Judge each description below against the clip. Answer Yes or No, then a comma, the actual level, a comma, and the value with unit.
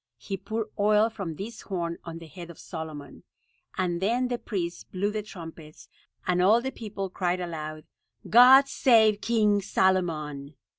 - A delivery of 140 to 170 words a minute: Yes, average, 155 wpm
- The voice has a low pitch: No, high, 190 Hz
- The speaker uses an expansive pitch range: No, average, 4.4 semitones